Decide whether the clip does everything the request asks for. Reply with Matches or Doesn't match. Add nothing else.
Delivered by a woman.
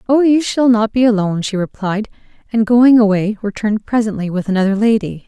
Matches